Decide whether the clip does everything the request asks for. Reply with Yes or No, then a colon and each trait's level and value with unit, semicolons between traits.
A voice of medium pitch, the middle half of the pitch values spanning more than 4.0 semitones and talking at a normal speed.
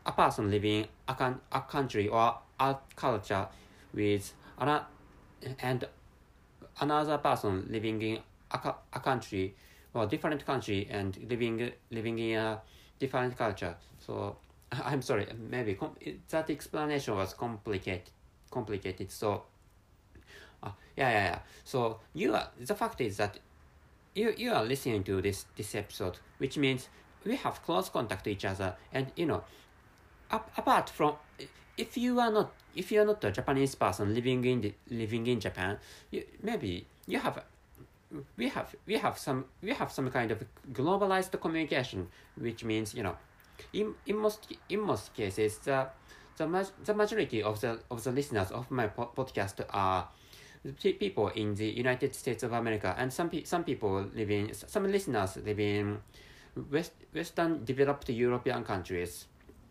No: low, 115 Hz; average, 5.0 semitones; average, 160 wpm